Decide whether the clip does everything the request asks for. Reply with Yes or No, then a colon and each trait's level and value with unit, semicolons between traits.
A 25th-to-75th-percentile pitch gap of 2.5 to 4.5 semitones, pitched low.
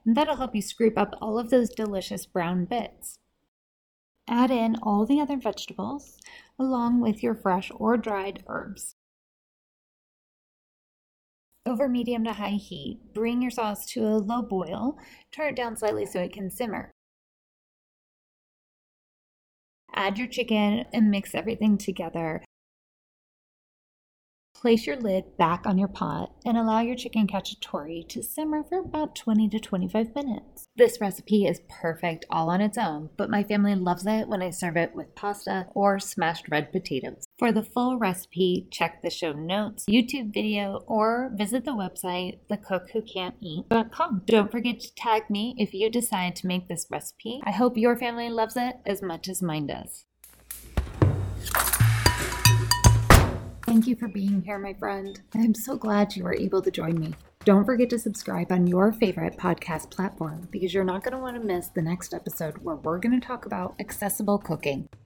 No: average, 4.2 semitones; high, 205 Hz